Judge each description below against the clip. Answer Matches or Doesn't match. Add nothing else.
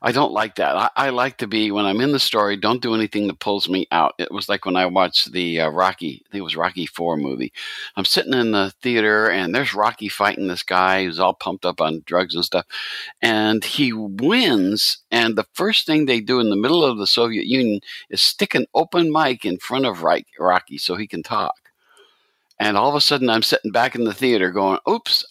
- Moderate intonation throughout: Matches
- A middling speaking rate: Doesn't match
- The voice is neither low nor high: Doesn't match